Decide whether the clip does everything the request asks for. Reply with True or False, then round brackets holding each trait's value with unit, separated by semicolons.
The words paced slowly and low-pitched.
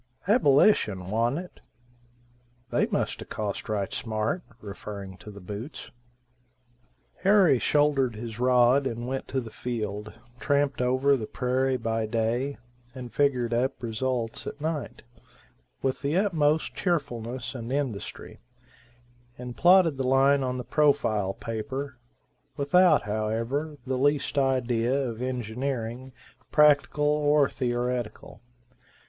True (120 wpm; 130 Hz)